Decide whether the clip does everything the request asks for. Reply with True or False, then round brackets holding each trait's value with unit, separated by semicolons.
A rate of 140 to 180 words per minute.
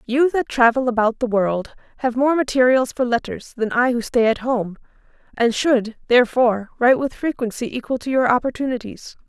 True (175 wpm)